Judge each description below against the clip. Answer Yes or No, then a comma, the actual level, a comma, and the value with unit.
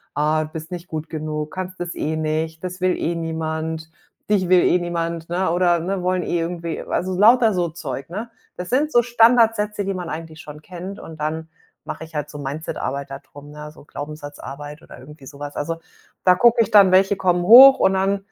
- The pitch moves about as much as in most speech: Yes, average, 3.3 semitones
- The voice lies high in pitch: No, medium, 170 Hz